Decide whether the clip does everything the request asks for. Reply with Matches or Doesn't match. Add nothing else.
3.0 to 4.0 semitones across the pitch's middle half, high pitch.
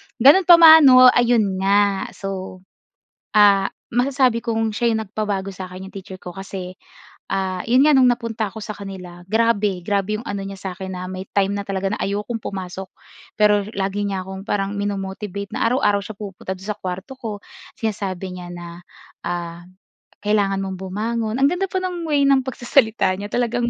Matches